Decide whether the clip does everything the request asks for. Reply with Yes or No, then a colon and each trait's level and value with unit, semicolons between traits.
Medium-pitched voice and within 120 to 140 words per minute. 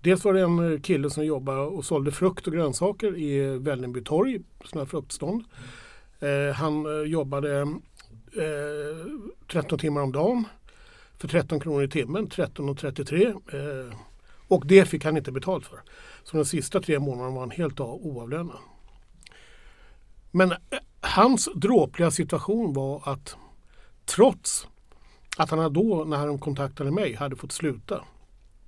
Yes: medium, 150 Hz; average, 130 wpm